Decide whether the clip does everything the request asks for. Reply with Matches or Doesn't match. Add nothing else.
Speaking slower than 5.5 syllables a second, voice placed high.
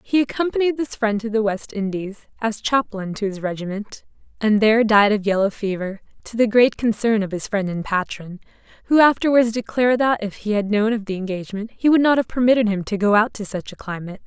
Doesn't match